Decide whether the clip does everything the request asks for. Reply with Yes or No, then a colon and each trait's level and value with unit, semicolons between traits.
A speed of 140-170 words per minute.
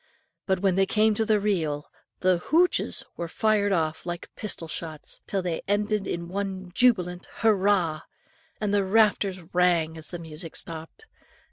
Yes: average, 155 wpm